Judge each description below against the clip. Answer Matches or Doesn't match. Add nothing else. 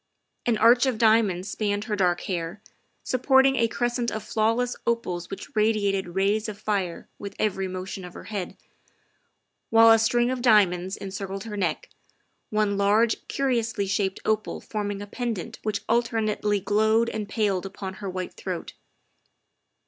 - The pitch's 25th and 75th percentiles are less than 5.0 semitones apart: Matches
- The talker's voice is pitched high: Matches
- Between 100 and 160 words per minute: Matches